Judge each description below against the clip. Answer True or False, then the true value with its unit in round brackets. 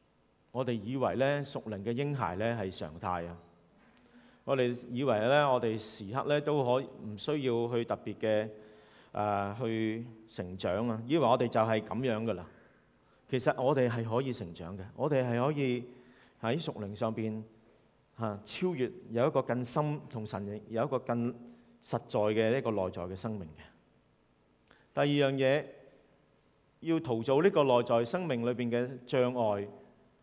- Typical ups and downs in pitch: True (3.4 semitones)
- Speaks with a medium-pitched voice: False (115 Hz)